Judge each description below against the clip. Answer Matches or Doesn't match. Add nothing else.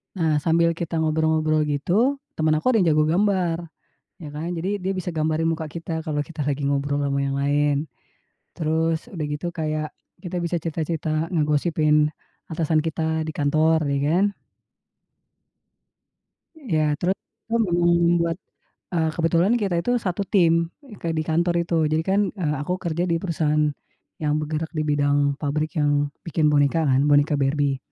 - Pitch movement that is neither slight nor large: Doesn't match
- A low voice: Doesn't match